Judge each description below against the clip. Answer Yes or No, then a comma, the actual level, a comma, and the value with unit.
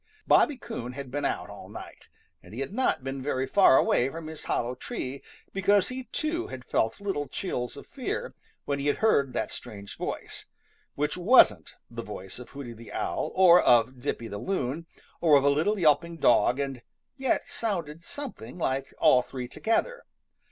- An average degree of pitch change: No, wide, 7.0 semitones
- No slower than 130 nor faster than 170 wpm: No, average, 180 wpm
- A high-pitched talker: No, medium, 140 Hz